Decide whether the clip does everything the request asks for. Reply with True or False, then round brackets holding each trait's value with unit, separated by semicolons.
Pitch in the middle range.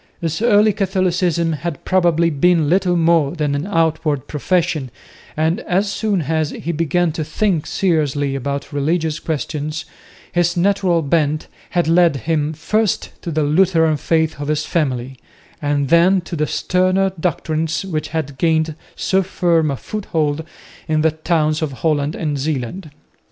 True (160 Hz)